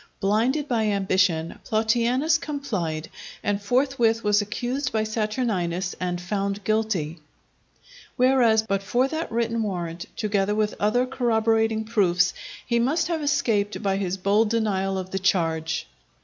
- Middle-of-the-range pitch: No, high, 215 Hz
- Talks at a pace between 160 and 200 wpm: No, slow, 135 wpm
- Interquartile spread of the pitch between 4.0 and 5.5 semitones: No, average, 3.5 semitones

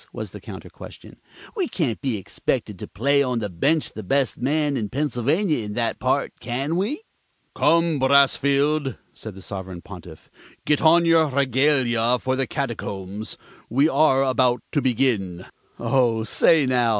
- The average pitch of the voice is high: No, low, 130 Hz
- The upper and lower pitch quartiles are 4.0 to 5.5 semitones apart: Yes, average, 4.6 semitones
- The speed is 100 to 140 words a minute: No, average, 155 wpm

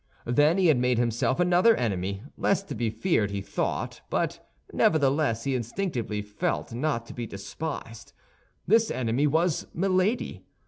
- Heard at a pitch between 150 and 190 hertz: No, low, 130 Hz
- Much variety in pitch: Yes, wide, 7.2 semitones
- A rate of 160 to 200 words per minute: No, average, 145 wpm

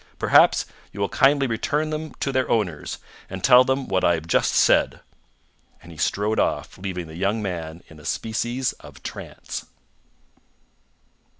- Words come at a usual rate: Yes, average, 160 wpm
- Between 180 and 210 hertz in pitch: No, low, 105 Hz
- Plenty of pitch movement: Yes, wide, 7.0 semitones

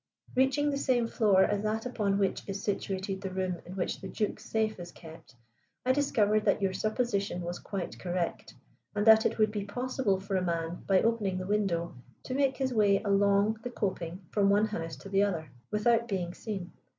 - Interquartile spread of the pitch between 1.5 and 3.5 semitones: Yes, average, 2.8 semitones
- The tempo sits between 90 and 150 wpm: No, average, 200 wpm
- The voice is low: No, high, 200 Hz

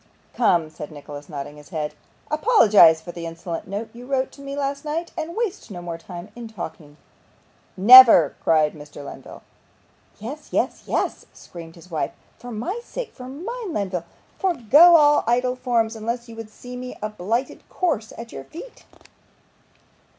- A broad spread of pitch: Yes, wide, 8.6 semitones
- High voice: Yes, high, 225 Hz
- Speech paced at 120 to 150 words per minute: No, average, 165 wpm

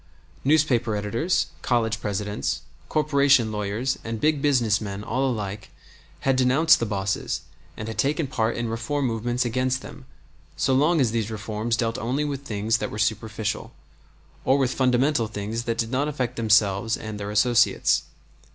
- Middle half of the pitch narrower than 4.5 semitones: Yes, average, 3.6 semitones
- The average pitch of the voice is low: Yes, low, 115 Hz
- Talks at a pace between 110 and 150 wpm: No, average, 160 wpm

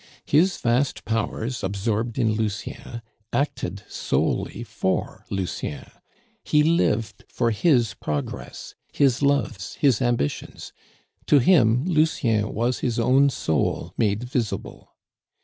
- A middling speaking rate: No, slow, 110 wpm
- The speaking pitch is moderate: No, low, 120 Hz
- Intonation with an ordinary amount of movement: Yes, average, 4.3 semitones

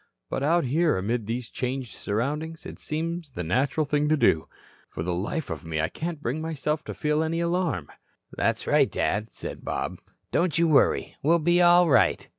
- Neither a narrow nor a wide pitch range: No, wide, 6.0 semitones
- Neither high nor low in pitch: Yes, medium, 150 Hz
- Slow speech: No, average, 190 wpm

